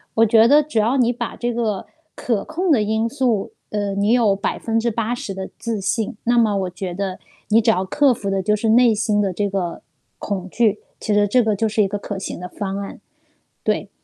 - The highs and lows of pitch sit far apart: No, average, 2.8 semitones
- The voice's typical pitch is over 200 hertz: Yes, high, 215 Hz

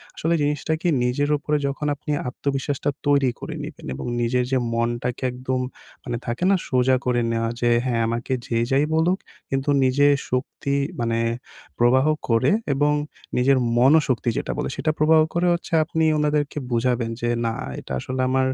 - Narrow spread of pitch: No, average, 3.2 semitones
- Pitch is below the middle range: Yes, low, 130 Hz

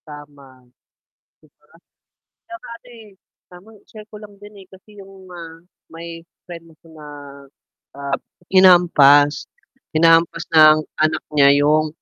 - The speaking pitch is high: No, medium, 165 Hz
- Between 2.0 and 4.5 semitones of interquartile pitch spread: Yes, average, 4.1 semitones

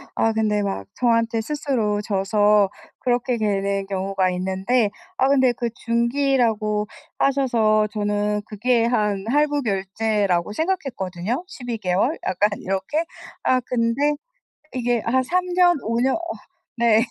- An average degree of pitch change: Yes, average, 3.6 semitones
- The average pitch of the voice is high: Yes, high, 225 Hz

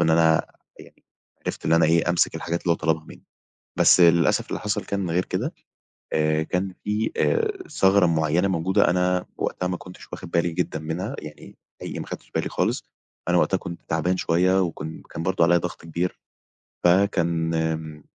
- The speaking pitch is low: Yes, very low, 85 Hz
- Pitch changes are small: Yes, narrow, 2.1 semitones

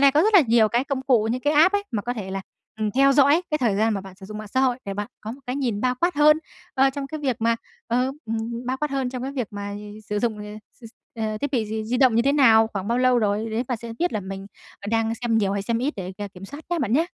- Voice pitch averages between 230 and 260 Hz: Yes, high, 235 Hz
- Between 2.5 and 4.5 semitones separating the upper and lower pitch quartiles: Yes, average, 4.0 semitones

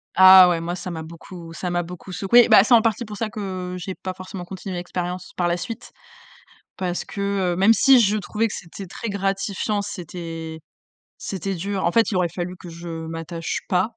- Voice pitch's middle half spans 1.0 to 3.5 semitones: Yes, narrow, 2.5 semitones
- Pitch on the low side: No, medium, 185 Hz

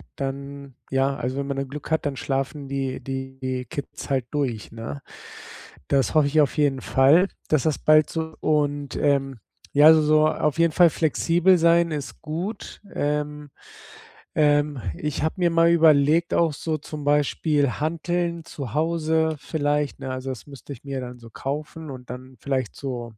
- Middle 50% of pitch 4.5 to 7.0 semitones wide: No, average, 2.7 semitones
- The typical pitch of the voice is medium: Yes, medium, 145 Hz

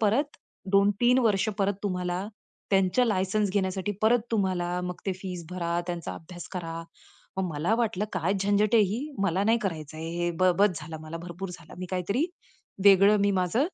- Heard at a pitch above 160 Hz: Yes, high, 190 Hz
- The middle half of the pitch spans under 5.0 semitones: Yes, average, 2.8 semitones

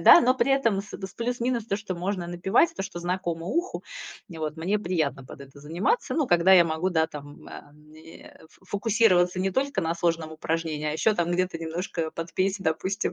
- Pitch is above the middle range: No, medium, 175 Hz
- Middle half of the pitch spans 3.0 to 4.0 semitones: Yes, average, 3.7 semitones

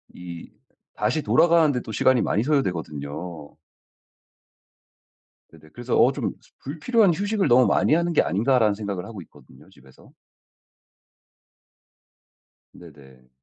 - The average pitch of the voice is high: No, low, 110 Hz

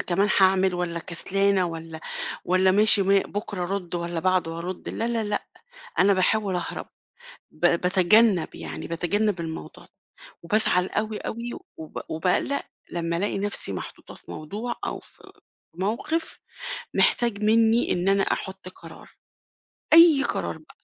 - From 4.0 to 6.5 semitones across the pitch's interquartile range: No, average, 3.4 semitones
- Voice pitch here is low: No, high, 190 Hz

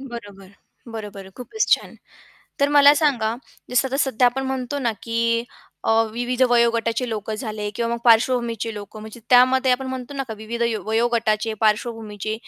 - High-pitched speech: Yes, high, 235 Hz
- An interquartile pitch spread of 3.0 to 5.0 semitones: No, narrow, 2.5 semitones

